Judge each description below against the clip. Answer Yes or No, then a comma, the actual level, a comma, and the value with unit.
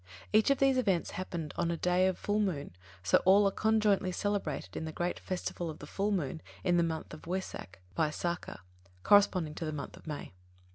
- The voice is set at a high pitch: No, medium, 180 Hz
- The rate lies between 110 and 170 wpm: No, average, 195 wpm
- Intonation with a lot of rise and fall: No, average, 4.1 semitones